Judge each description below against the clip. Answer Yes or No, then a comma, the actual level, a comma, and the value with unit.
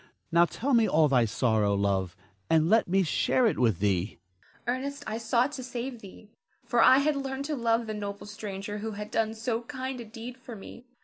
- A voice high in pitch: Yes, high, 220 Hz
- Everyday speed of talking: No, fast, 210 wpm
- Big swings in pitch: Yes, wide, 6.6 semitones